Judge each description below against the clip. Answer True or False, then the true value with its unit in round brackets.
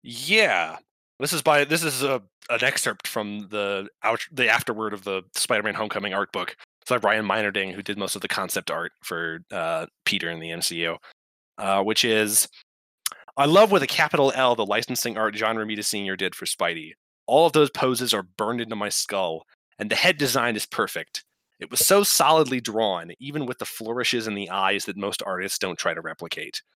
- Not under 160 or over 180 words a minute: False (200 wpm)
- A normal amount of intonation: False (5.7 semitones)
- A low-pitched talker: True (110 Hz)